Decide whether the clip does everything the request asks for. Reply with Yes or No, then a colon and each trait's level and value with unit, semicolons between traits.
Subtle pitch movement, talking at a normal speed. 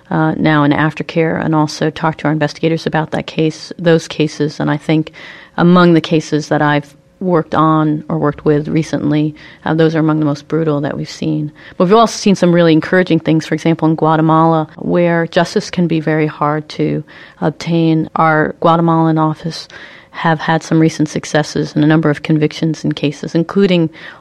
Yes: narrow, 1.5 semitones; average, 185 wpm